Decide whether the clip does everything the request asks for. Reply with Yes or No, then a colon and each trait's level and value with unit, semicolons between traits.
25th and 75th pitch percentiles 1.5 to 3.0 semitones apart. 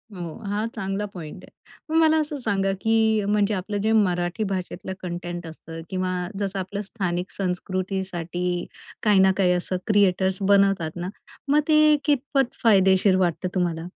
Yes: average, 2.7 semitones